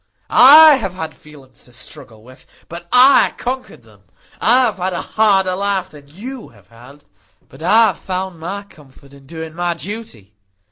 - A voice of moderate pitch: Yes, medium, 175 Hz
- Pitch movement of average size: No, wide, 7.0 semitones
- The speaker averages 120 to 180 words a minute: Yes, average, 175 wpm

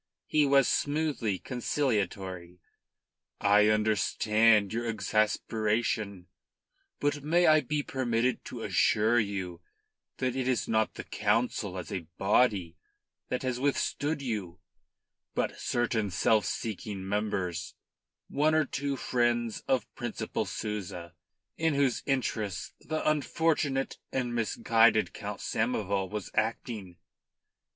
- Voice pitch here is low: Yes, low, 110 Hz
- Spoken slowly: Yes, slow, 110 wpm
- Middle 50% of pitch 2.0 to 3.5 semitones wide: No, average, 4.6 semitones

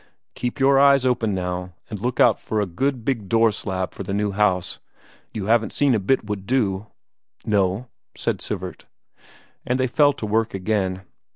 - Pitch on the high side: No, low, 110 Hz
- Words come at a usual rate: Yes, average, 180 wpm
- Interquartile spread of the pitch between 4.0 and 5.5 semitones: Yes, average, 4.4 semitones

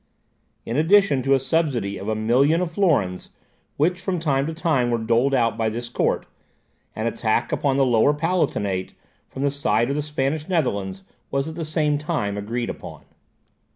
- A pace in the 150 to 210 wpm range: Yes, average, 180 wpm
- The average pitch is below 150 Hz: Yes, low, 135 Hz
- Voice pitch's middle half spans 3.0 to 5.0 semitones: No, wide, 5.4 semitones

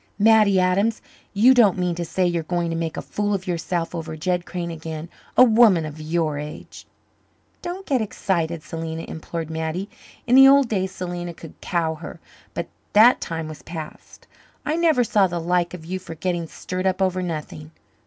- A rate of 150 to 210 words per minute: Yes, average, 185 wpm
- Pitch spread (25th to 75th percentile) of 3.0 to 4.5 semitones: Yes, average, 3.6 semitones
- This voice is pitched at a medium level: Yes, medium, 175 Hz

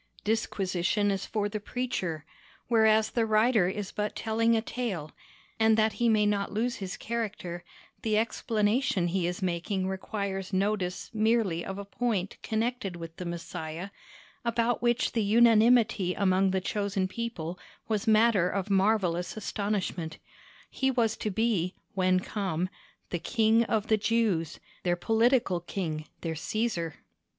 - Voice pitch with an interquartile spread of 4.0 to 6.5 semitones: No, average, 3.5 semitones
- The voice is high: Yes, high, 205 Hz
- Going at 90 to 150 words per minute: Yes, average, 140 wpm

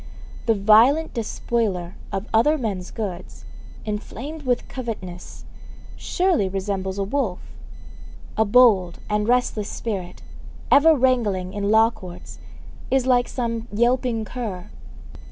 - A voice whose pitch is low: No, high, 220 Hz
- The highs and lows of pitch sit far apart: No, average, 4.2 semitones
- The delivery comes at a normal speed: No, slow, 115 wpm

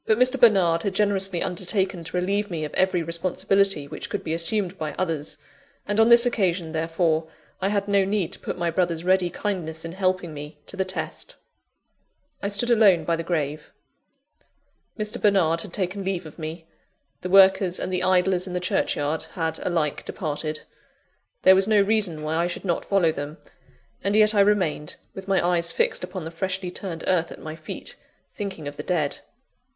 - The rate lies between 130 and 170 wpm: No, average, 190 wpm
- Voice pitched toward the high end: No, medium, 180 Hz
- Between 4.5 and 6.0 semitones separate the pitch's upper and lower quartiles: No, average, 3.2 semitones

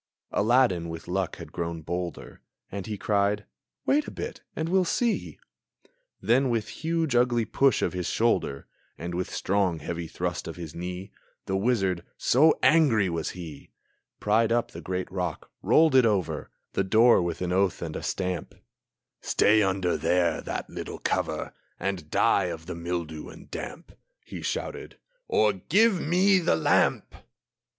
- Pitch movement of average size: No, wide, 5.7 semitones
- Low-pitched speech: Yes, very low, 95 Hz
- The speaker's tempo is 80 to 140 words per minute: No, average, 160 wpm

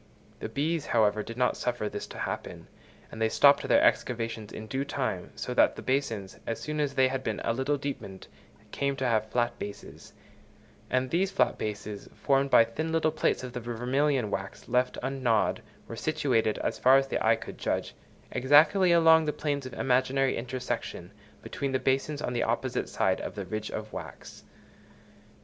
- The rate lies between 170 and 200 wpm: Yes, average, 185 wpm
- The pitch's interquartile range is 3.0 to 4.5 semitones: Yes, average, 3.7 semitones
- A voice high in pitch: No, low, 130 Hz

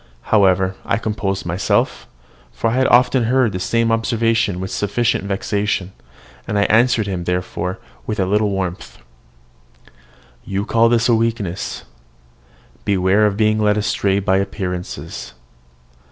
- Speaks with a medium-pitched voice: No, low, 105 Hz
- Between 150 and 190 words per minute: No, slow, 135 wpm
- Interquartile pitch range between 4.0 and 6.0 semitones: No, average, 3.0 semitones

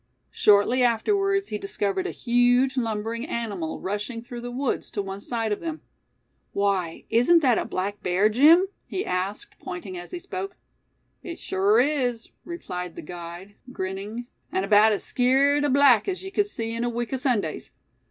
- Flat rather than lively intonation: No, average, 5.1 semitones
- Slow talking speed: No, average, 170 wpm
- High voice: Yes, high, 230 Hz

